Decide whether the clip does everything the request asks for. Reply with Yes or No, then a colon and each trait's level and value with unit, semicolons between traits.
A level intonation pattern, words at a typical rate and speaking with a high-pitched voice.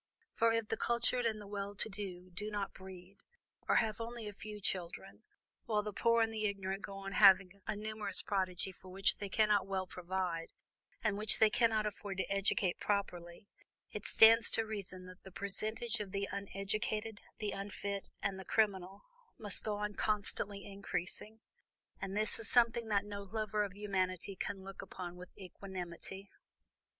Yes: narrow, 2.0 semitones; average, 175 wpm; high, 200 Hz